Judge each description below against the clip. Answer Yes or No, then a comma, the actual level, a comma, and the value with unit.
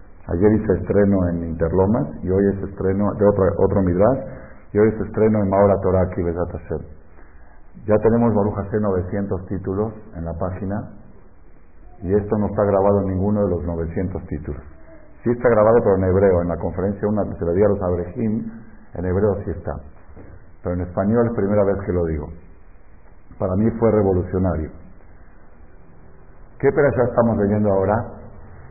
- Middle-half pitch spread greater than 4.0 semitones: No, average, 3.3 semitones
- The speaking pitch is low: Yes, very low, 95 Hz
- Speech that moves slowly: No, average, 165 wpm